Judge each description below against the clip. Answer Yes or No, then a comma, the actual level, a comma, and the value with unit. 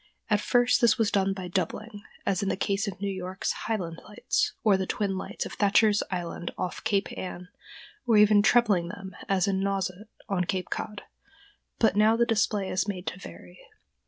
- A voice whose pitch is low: No, high, 195 Hz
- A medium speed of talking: Yes, average, 190 wpm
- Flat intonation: Yes, narrow, 2.2 semitones